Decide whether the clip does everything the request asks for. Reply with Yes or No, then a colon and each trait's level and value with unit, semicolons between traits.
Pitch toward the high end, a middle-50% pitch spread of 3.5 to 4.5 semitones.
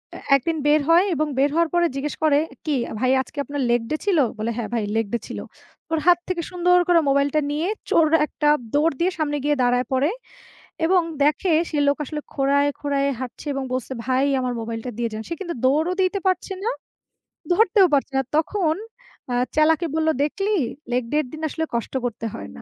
Yes: very high, 295 Hz; average, 4.2 semitones